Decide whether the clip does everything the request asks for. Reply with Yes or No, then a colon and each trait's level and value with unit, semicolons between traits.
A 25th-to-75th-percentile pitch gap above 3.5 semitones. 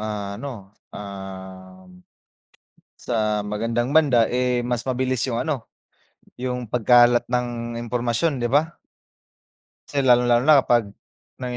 No: average, 2.9 semitones